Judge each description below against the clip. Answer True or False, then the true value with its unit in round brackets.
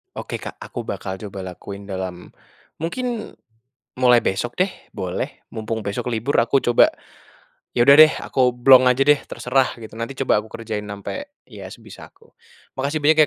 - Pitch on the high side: False (120 Hz)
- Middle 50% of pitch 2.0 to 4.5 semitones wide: False (5.0 semitones)